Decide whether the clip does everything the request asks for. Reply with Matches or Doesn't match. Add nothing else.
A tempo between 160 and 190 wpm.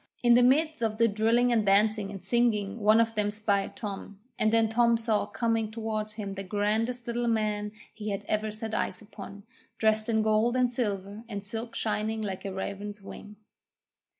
Matches